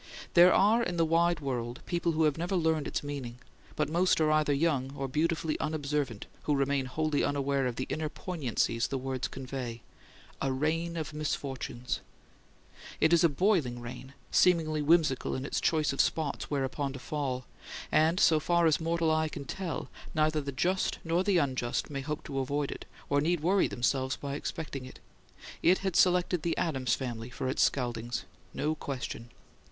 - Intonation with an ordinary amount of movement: Yes, average, 3.8 semitones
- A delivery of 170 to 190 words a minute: Yes, average, 180 wpm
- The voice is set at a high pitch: No, medium, 150 Hz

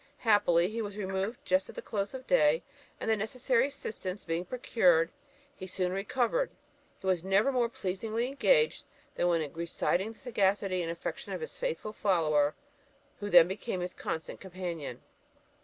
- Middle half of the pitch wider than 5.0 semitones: No, average, 4.4 semitones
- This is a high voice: Yes, high, 195 Hz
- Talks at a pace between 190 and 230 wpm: No, average, 160 wpm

